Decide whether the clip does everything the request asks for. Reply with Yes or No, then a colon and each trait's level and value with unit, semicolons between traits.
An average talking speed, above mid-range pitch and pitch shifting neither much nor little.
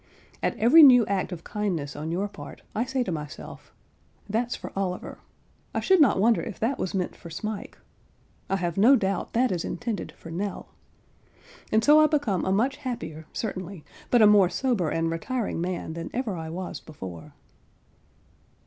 No: average, 175 wpm; high, 195 Hz; wide, 5.8 semitones